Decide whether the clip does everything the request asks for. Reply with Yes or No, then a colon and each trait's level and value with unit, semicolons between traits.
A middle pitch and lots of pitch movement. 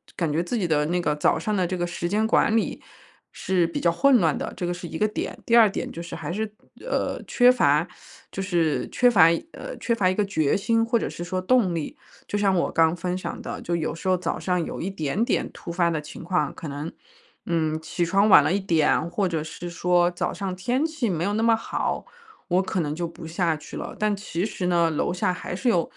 No: medium, 180 Hz; average, 3.5 semitones